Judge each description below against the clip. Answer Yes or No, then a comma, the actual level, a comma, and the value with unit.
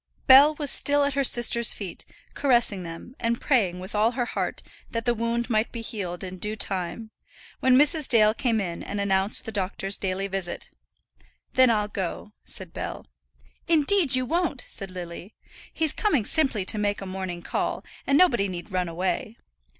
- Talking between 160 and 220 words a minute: Yes, average, 175 wpm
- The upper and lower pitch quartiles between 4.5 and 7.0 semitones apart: Yes, average, 5.1 semitones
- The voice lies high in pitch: Yes, high, 215 Hz